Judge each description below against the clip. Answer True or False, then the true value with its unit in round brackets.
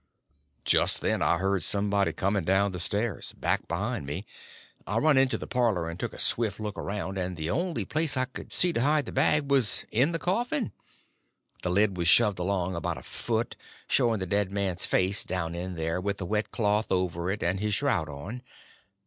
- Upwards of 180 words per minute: True (200 wpm)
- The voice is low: True (100 Hz)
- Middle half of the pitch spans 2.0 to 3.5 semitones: False (4.7 semitones)